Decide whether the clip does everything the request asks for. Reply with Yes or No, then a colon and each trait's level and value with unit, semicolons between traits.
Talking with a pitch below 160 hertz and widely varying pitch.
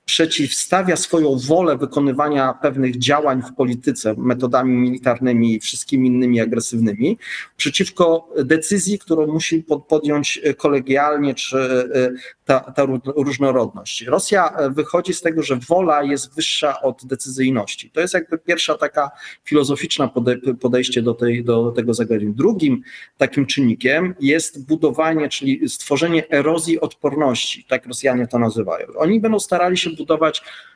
No: medium, 140 Hz; average, 3.9 semitones